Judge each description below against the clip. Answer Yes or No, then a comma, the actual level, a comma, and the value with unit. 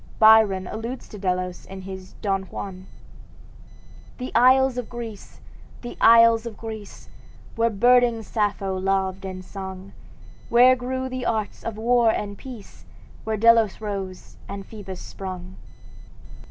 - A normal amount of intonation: Yes, average, 3.4 semitones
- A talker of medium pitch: No, high, 215 Hz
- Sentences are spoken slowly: Yes, slow, 130 wpm